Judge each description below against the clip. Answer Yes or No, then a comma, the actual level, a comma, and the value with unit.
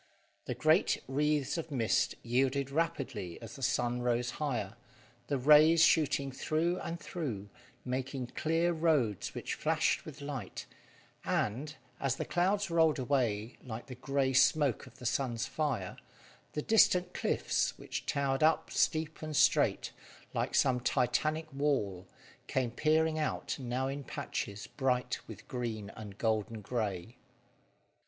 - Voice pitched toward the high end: No, low, 135 Hz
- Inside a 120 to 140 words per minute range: Yes, slow, 135 wpm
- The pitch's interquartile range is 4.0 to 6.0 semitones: Yes, average, 4.4 semitones